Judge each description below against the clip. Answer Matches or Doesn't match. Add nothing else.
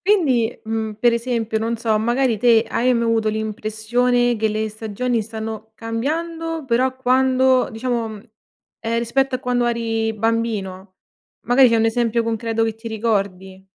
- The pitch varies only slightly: Matches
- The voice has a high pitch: Matches